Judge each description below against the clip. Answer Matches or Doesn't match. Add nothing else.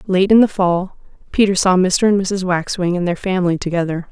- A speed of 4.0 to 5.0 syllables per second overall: Doesn't match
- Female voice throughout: Matches